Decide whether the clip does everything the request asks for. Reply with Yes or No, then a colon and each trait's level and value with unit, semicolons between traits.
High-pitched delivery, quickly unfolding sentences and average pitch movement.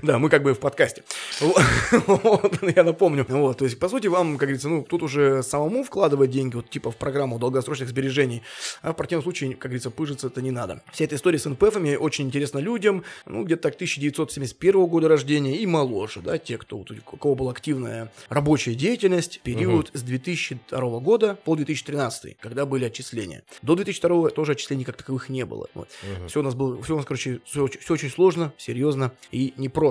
No: medium, 140 Hz; fast, 185 wpm; average, 4.1 semitones